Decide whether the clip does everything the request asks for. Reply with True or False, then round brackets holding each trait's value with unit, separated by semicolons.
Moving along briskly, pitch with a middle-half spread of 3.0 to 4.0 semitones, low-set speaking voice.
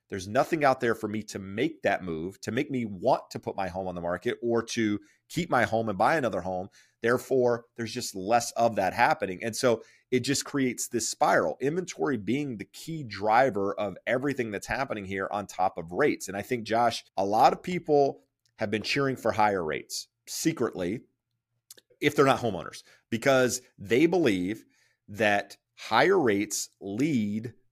False (180 wpm; 3.5 semitones; 115 Hz)